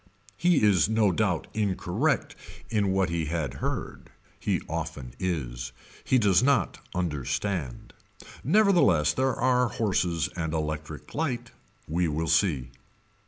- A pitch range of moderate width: No, wide, 6.4 semitones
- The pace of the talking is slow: Yes, slow, 120 wpm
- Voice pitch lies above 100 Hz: No, very low, 90 Hz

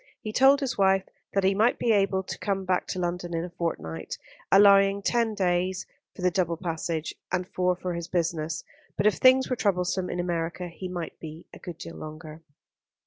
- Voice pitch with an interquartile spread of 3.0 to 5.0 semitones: No, narrow, 2.6 semitones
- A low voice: No, medium, 180 Hz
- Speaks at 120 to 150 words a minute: No, average, 195 wpm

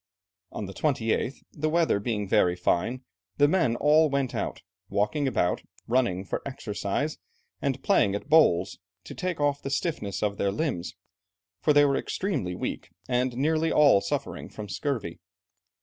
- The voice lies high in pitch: No, low, 130 Hz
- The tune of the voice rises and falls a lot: Yes, wide, 6.6 semitones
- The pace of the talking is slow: No, average, 155 wpm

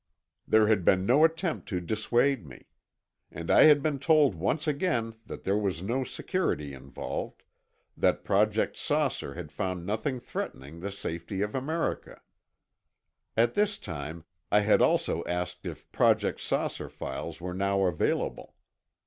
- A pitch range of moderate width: No, wide, 7.7 semitones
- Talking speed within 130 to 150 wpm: Yes, average, 145 wpm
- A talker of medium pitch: No, low, 105 Hz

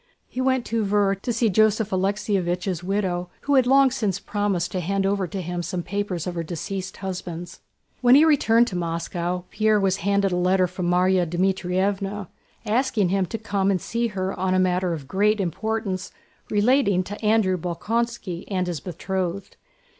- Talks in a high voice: Yes, high, 195 Hz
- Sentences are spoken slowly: No, average, 175 wpm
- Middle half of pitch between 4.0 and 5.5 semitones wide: No, average, 2.8 semitones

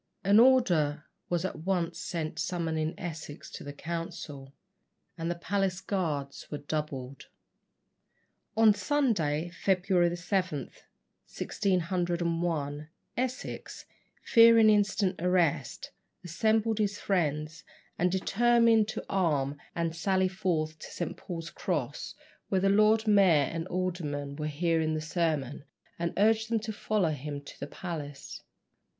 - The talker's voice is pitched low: No, medium, 175 Hz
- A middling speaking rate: No, slow, 120 wpm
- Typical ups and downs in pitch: Yes, average, 4.1 semitones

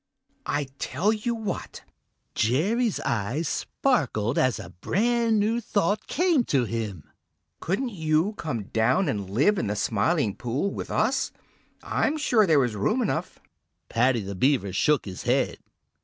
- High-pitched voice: No, medium, 150 Hz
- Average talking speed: Yes, average, 145 wpm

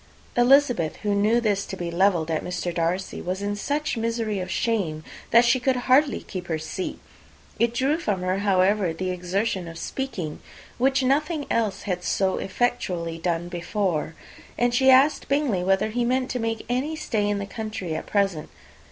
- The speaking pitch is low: No, high, 205 Hz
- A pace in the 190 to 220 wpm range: No, average, 180 wpm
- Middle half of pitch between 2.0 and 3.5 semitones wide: No, average, 5.3 semitones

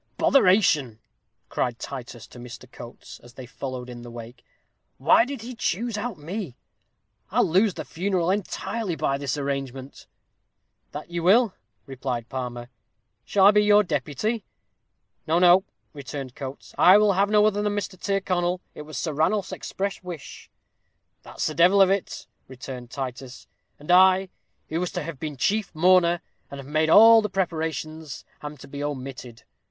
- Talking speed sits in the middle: Yes, average, 160 wpm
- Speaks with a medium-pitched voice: Yes, medium, 160 Hz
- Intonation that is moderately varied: No, wide, 6.5 semitones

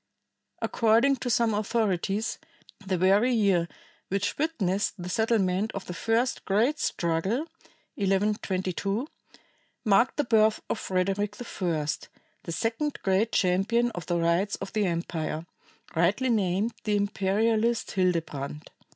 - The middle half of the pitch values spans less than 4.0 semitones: Yes, average, 3.6 semitones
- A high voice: Yes, high, 200 Hz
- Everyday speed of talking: No, slow, 120 wpm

